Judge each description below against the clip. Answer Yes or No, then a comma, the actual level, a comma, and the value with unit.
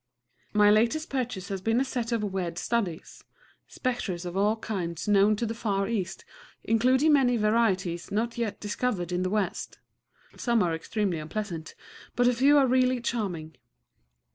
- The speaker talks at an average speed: Yes, average, 160 wpm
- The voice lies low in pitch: No, high, 215 Hz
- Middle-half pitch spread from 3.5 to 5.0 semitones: Yes, average, 4.3 semitones